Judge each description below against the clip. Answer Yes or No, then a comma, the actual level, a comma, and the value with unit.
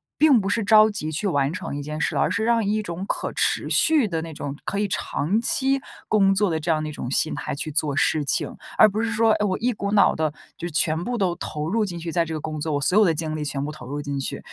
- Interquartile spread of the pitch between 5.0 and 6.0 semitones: Yes, wide, 5.6 semitones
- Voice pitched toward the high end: No, medium, 170 Hz